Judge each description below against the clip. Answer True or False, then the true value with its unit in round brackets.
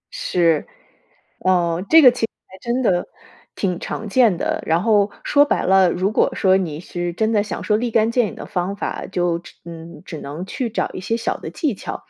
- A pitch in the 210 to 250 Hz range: False (190 Hz)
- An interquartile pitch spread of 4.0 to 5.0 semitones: True (4.4 semitones)